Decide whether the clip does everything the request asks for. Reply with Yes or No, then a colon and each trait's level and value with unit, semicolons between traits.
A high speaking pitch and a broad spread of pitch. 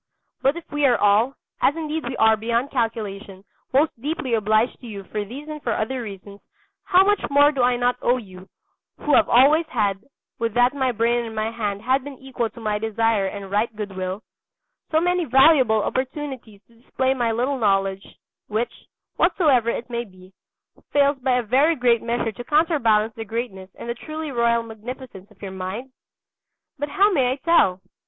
No: high, 235 Hz; average, 4.2 semitones